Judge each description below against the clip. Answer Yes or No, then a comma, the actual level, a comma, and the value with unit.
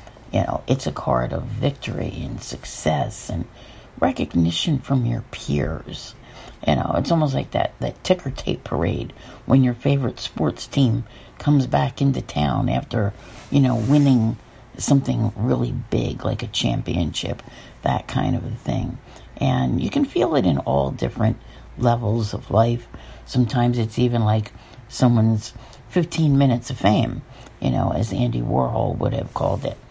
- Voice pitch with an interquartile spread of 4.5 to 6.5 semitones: No, average, 3.5 semitones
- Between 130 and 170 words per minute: Yes, average, 155 wpm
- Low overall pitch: Yes, low, 120 Hz